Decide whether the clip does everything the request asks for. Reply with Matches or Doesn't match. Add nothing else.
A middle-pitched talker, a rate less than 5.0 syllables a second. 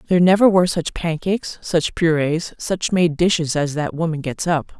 Doesn't match